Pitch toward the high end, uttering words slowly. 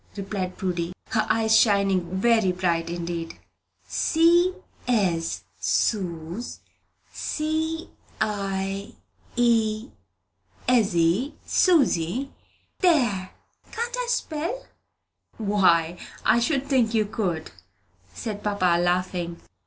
Yes: high, 205 Hz; slow, 85 wpm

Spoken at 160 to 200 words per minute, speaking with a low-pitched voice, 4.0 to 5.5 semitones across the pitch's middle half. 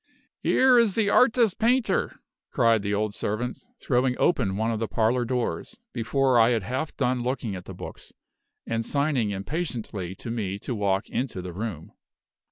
Yes: average, 170 wpm; low, 120 Hz; average, 4.8 semitones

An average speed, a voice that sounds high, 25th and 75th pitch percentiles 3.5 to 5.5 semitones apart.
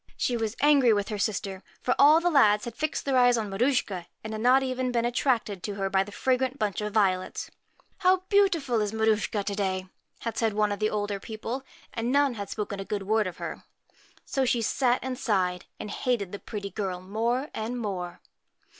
No: fast, 215 wpm; high, 220 Hz; average, 3.9 semitones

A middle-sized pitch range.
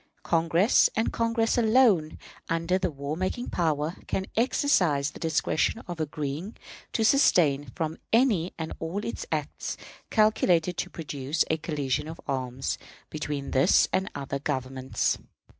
Yes: average, 4.9 semitones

